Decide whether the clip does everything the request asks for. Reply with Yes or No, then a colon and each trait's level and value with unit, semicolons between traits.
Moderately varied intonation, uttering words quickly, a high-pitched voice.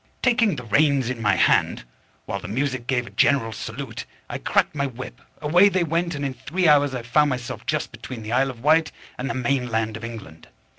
No: average, 4.2 semitones; fast, 225 wpm; low, 130 Hz